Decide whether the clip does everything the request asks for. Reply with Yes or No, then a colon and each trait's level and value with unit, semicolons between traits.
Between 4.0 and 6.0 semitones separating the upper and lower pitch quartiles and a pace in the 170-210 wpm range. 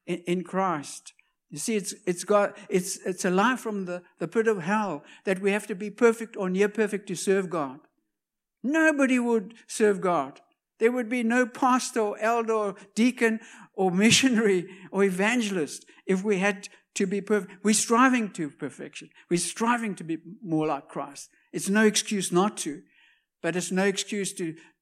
No: average, 3.3 semitones; average, 175 wpm